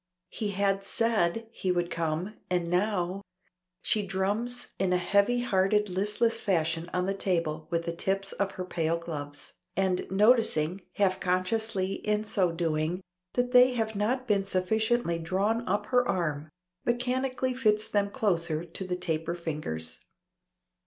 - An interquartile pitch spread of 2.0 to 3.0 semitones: No, average, 4.0 semitones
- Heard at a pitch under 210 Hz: Yes, high, 190 Hz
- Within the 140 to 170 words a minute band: Yes, average, 145 wpm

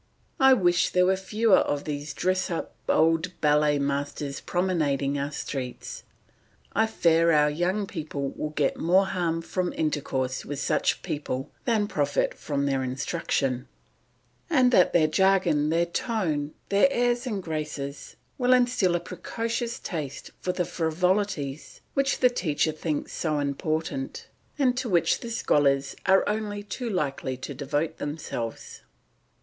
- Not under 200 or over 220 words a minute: No, average, 145 wpm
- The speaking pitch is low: No, medium, 165 Hz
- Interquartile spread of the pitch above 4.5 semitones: Yes, wide, 5.4 semitones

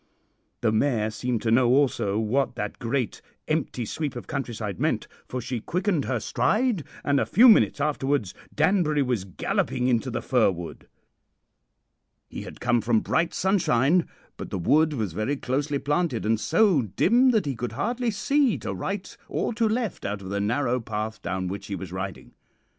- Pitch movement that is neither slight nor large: No, wide, 6.6 semitones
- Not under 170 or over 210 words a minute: Yes, average, 175 wpm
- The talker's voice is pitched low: Yes, low, 130 Hz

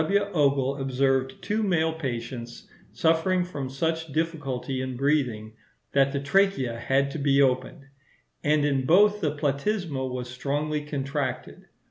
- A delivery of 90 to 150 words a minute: Yes, slow, 135 wpm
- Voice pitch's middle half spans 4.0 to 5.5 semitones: No, average, 3.5 semitones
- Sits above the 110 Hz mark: Yes, medium, 140 Hz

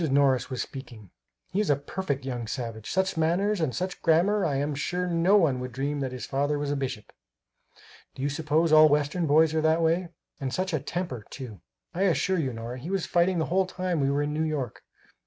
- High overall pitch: No, medium, 150 Hz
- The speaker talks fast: Yes, fast, 220 wpm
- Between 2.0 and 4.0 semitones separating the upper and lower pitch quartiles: No, average, 4.5 semitones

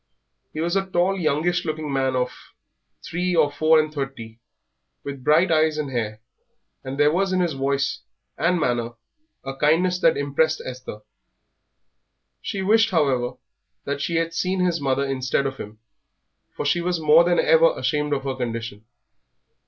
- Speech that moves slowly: No, average, 160 wpm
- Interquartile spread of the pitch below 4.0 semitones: No, average, 4.3 semitones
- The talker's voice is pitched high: No, medium, 150 Hz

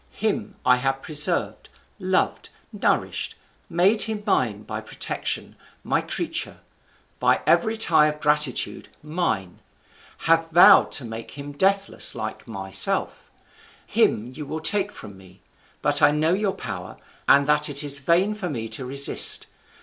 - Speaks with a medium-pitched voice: Yes, medium, 150 Hz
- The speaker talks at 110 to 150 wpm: Yes, average, 140 wpm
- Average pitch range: No, wide, 6.0 semitones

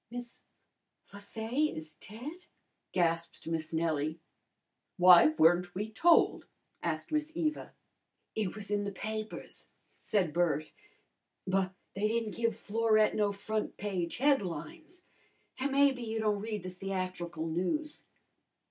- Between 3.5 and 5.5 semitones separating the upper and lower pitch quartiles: Yes, average, 4.7 semitones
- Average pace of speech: No, slow, 125 wpm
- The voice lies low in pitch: No, high, 205 Hz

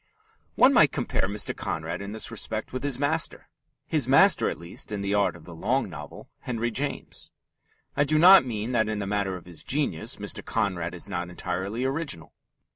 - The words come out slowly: No, average, 195 wpm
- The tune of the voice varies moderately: No, wide, 6.7 semitones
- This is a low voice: Yes, low, 110 Hz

